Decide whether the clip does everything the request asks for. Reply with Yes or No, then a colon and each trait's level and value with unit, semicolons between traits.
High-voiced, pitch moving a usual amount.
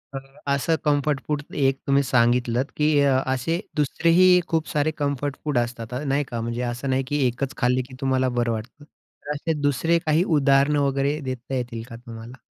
No: low, 135 Hz; average, 3.0 semitones